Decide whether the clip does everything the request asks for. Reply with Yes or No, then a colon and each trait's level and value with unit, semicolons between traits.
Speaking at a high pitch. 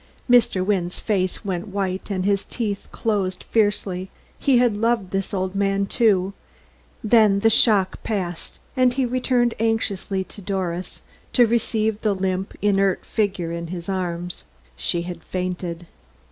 Yes: high, 195 Hz